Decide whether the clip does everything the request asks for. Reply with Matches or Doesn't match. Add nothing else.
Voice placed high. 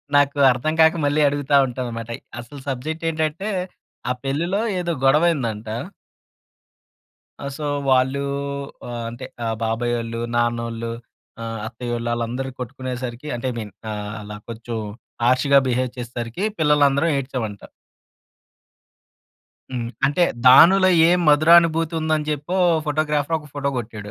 Doesn't match